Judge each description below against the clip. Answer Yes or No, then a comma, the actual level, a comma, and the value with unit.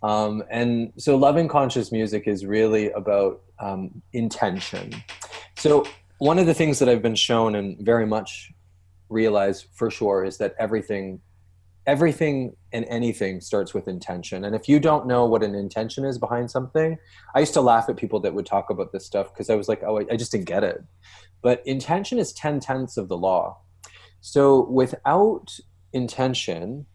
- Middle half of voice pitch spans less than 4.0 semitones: No, average, 5.3 semitones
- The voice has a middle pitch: No, low, 110 Hz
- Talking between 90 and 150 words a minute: No, average, 180 wpm